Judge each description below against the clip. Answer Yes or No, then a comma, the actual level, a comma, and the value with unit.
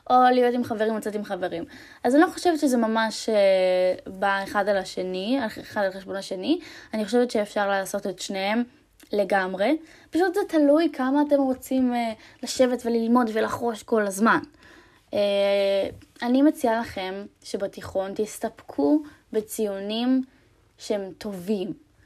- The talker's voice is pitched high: Yes, high, 225 Hz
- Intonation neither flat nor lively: Yes, average, 4.9 semitones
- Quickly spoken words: No, average, 130 wpm